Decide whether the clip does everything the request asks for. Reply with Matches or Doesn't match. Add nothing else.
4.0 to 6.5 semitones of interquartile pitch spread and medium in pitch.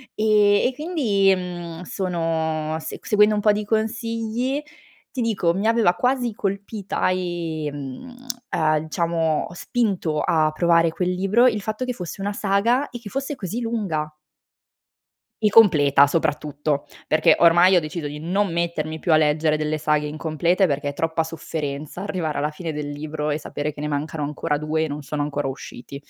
Matches